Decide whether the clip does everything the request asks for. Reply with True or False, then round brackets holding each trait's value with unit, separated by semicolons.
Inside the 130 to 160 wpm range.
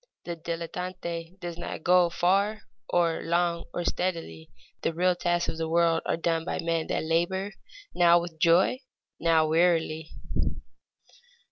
True (140 wpm)